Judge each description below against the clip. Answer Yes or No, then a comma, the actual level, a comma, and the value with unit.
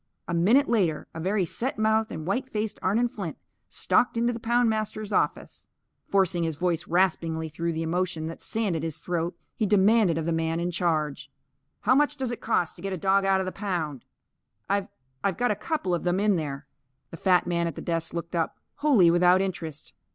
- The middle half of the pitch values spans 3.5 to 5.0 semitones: Yes, average, 4.4 semitones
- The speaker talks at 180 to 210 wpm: Yes, fast, 205 wpm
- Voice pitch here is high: No, medium, 180 Hz